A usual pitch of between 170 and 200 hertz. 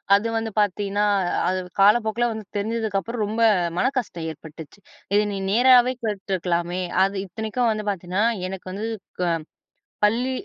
No: high, 210 Hz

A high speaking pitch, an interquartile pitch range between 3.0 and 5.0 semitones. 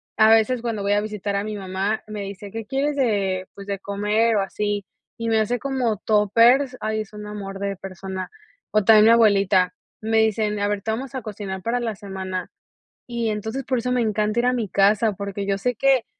No: high, 210 Hz; narrow, 2.4 semitones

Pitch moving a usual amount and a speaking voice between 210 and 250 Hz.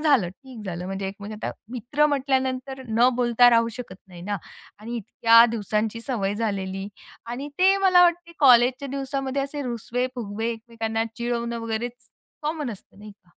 Yes: average, 3.8 semitones; high, 235 Hz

